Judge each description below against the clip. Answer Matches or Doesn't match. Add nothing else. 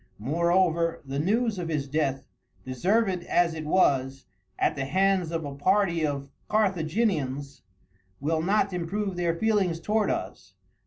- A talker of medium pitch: Matches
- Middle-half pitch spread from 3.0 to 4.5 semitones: Doesn't match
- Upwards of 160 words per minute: Doesn't match